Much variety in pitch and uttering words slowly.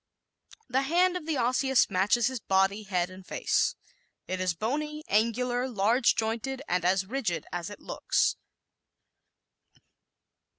Yes: wide, 5.7 semitones; slow, 130 wpm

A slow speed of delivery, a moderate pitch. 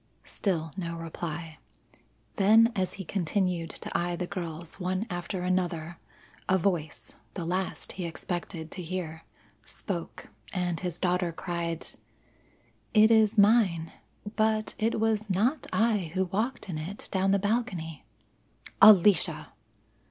Yes: slow, 130 wpm; medium, 180 Hz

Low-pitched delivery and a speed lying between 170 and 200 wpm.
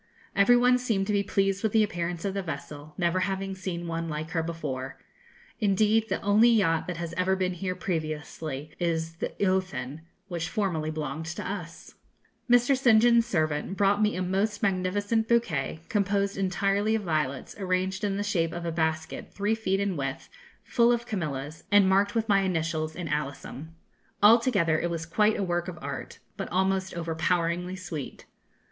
No: medium, 185 Hz; average, 175 wpm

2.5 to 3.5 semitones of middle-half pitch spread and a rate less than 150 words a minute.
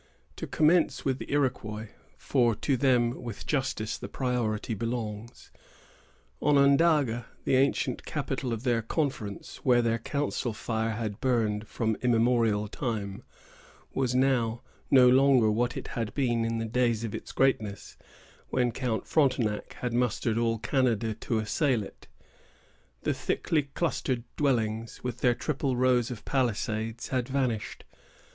Yes: average, 2.8 semitones; average, 140 wpm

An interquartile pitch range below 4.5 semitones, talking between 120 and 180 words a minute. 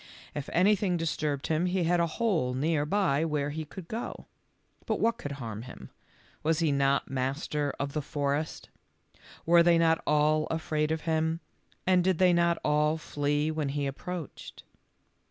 Yes: average, 3.0 semitones; average, 170 wpm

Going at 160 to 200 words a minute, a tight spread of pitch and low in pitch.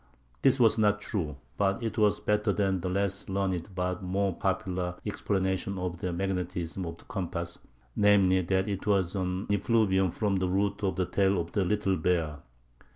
Yes: average, 170 wpm; narrow, 2.0 semitones; very low, 95 Hz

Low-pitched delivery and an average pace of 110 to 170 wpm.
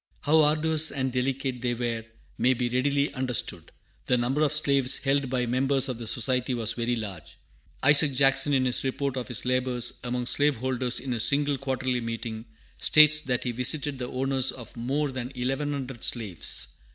No: low, 130 Hz; average, 180 wpm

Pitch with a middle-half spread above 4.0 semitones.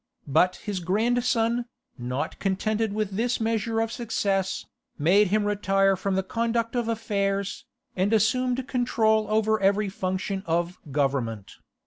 No: average, 3.1 semitones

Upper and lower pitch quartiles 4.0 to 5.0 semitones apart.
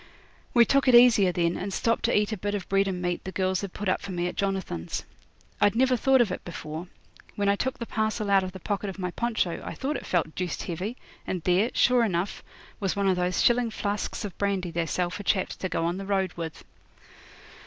No: average, 3.2 semitones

